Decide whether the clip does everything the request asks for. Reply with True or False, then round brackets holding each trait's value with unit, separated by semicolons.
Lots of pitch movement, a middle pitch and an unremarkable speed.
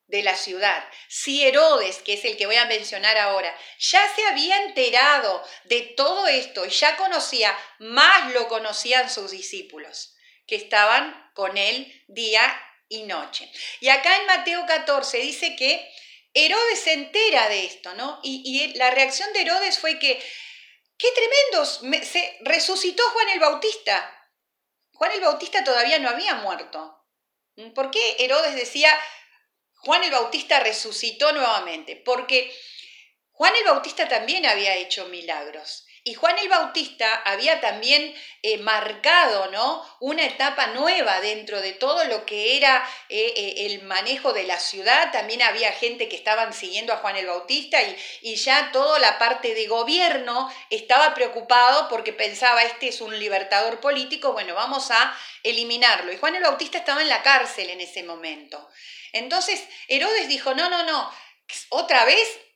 False (7.5 semitones; 265 Hz; 155 wpm)